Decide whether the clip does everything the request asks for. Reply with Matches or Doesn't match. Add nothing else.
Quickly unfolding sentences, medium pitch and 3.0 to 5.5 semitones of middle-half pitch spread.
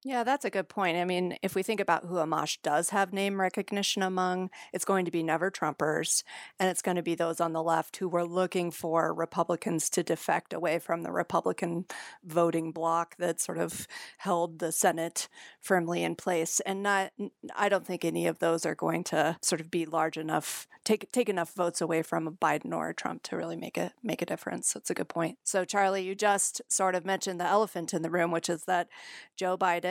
Doesn't match